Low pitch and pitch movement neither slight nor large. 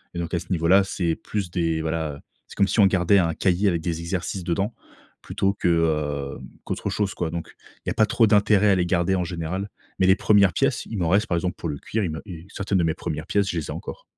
Yes: very low, 90 Hz; average, 3.1 semitones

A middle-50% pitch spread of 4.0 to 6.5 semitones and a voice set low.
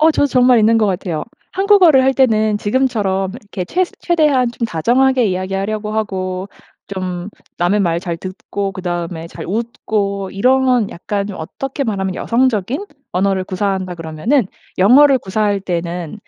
No: average, 5.1 semitones; high, 205 Hz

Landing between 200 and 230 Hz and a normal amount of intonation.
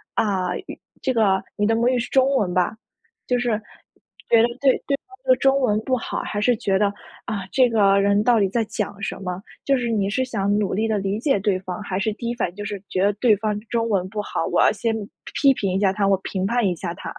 Yes: high, 210 Hz; average, 3.4 semitones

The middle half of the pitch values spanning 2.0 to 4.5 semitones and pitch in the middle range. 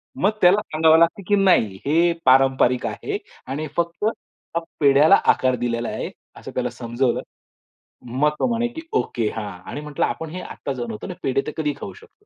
No: average, 5.3 semitones; medium, 150 Hz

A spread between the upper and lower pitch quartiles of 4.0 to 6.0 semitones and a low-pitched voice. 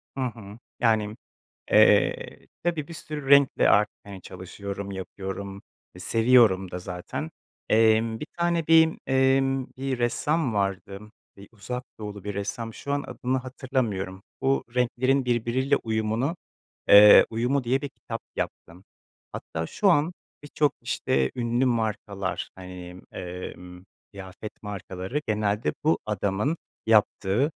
Yes: average, 5.2 semitones; low, 110 Hz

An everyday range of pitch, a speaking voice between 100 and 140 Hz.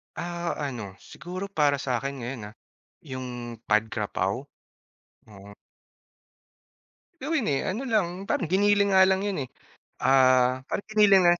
No: wide, 7.7 semitones; low, 135 Hz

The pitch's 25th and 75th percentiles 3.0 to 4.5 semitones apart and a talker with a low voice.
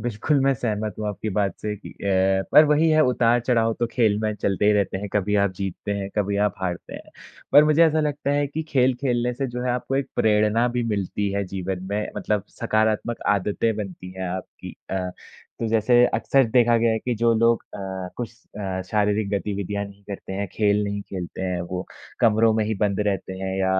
Yes: average, 3.3 semitones; low, 105 Hz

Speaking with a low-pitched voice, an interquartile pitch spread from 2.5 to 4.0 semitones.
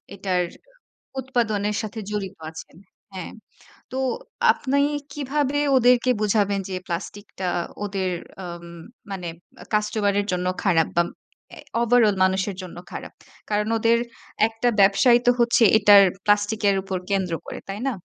No: high, 205 Hz; average, 3.2 semitones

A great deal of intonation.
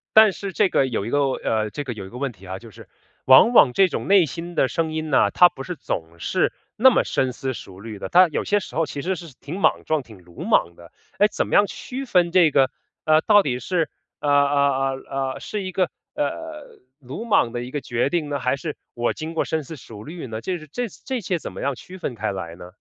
Yes: wide, 6.7 semitones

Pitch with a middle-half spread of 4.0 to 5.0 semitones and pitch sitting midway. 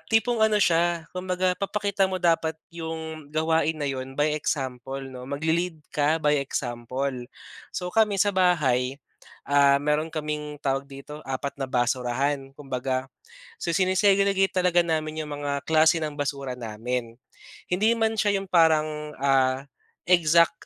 Yes: average, 4.6 semitones; medium, 155 Hz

